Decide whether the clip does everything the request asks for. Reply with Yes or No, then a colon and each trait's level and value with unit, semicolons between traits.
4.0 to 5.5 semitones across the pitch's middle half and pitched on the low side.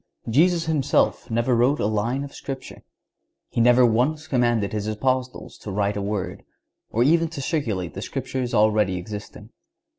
Yes: average, 4.3 semitones; low, 120 Hz